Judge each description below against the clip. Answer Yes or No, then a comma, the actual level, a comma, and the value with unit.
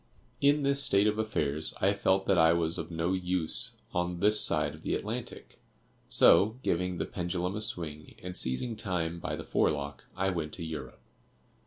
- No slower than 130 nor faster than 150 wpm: No, average, 180 wpm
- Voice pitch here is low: Yes, very low, 90 Hz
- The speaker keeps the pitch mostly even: No, average, 3.4 semitones